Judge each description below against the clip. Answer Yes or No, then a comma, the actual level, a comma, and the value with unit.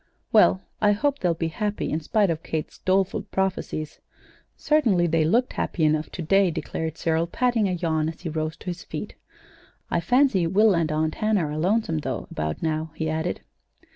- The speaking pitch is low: No, medium, 170 Hz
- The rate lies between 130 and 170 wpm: No, average, 185 wpm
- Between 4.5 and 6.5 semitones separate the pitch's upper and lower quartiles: No, average, 4.1 semitones